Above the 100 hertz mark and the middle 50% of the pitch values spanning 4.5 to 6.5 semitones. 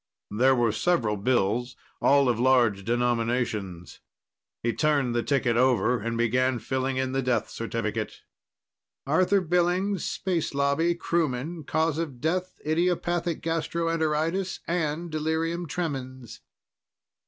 Yes: medium, 140 Hz; average, 5.3 semitones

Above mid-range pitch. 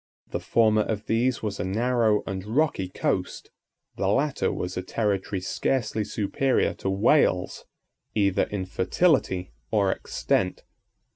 No: low, 105 Hz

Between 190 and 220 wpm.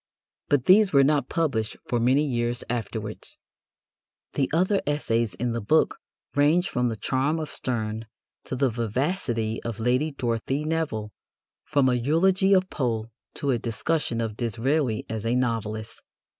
No: average, 150 wpm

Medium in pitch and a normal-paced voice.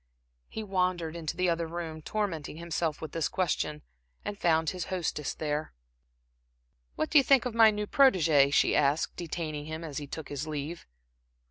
Yes: medium, 165 Hz; average, 170 wpm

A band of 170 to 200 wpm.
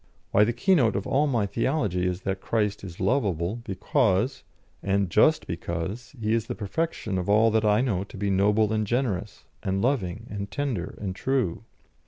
Yes: average, 180 wpm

